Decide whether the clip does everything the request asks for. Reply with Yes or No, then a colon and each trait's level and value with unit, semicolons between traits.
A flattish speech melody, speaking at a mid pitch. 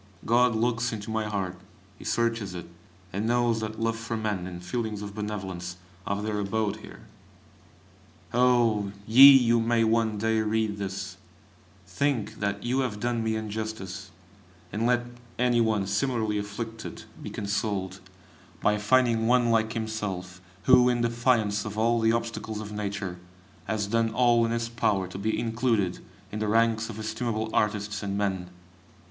No: narrow, 2.3 semitones; low, 110 Hz